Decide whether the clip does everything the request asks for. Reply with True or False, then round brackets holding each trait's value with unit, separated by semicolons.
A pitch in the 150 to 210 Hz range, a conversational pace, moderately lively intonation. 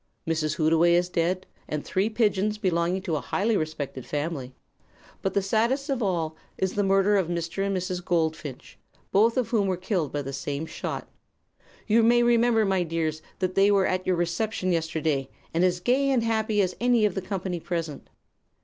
True (185 Hz; 185 wpm; 4.2 semitones)